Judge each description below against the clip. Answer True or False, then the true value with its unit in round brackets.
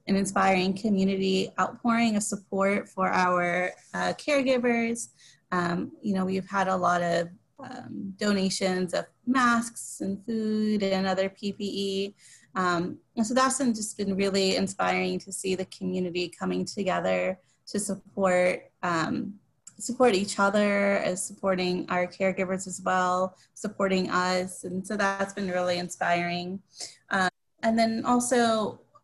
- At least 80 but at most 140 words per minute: True (135 wpm)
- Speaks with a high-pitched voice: True (195 Hz)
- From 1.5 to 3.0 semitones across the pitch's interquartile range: True (2.6 semitones)